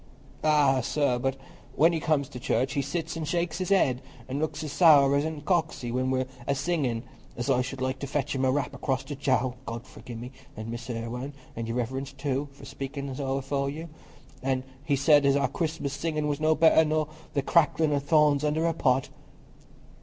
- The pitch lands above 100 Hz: Yes, medium, 140 Hz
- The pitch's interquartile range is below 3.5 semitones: Yes, average, 2.8 semitones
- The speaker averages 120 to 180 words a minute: No, fast, 205 wpm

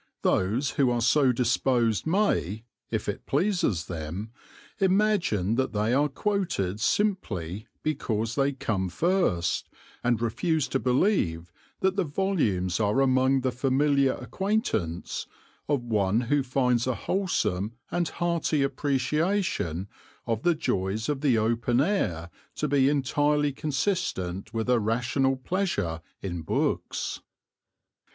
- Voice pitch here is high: No, low, 130 Hz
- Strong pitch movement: Yes, wide, 6.3 semitones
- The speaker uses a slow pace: Yes, slow, 125 wpm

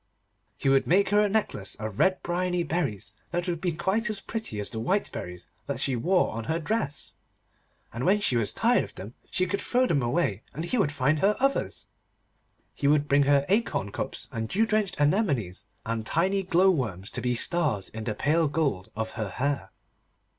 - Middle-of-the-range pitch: Yes, medium, 150 Hz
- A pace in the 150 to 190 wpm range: No, average, 200 wpm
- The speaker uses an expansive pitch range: Yes, wide, 8.7 semitones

